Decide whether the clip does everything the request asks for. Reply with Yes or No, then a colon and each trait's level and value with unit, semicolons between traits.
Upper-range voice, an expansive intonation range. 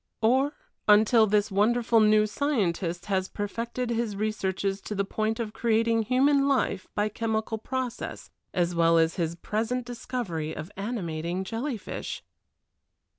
No: high, 215 Hz; average, 3.6 semitones